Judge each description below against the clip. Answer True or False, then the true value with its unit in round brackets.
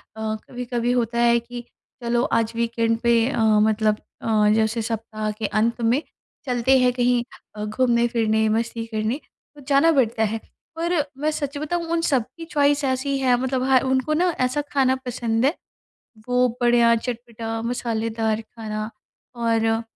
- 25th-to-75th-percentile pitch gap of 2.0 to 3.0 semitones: True (2.6 semitones)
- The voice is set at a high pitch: True (235 Hz)